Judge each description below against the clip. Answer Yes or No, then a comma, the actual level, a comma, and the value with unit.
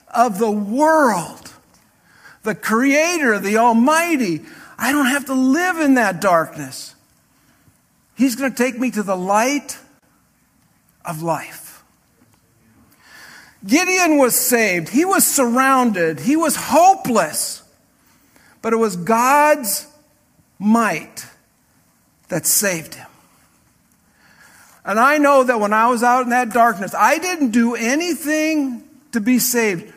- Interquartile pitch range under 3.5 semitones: No, average, 4.3 semitones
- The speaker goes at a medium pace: No, slow, 120 wpm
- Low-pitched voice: No, very high, 250 Hz